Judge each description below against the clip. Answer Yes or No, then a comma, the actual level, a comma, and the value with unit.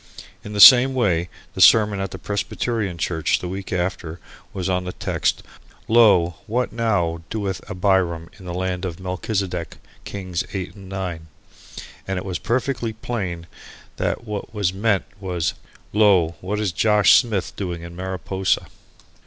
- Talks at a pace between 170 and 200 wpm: No, average, 155 wpm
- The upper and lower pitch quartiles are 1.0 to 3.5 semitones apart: Yes, average, 2.9 semitones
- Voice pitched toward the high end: No, very low, 95 Hz